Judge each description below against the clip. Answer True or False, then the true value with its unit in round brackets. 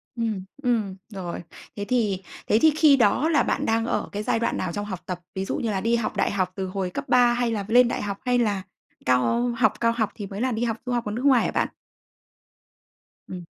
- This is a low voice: False (220 Hz)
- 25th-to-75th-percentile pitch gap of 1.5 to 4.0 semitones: True (3.7 semitones)